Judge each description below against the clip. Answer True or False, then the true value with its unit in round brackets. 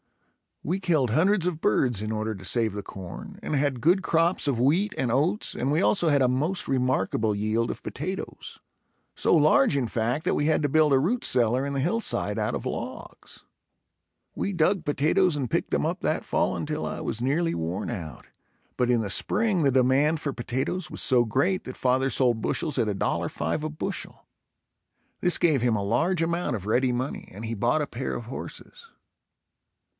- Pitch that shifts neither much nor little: False (5.7 semitones)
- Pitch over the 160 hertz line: False (135 Hz)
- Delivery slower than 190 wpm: False (195 wpm)